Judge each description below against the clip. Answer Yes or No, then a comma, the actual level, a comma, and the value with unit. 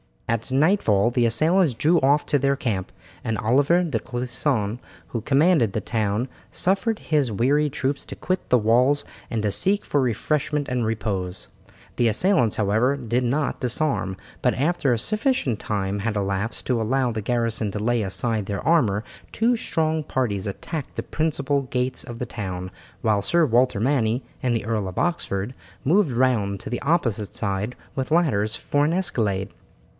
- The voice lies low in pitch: Yes, low, 125 Hz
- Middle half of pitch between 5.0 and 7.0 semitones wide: Yes, average, 5.3 semitones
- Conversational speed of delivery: Yes, average, 170 wpm